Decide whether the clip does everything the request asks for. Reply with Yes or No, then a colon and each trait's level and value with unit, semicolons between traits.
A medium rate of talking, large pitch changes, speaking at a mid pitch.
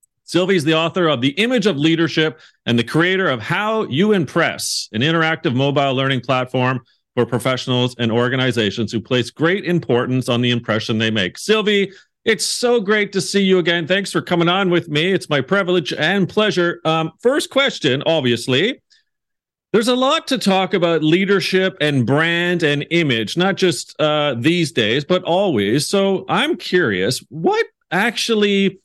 Yes: average, 165 wpm; wide, 6.7 semitones; medium, 165 Hz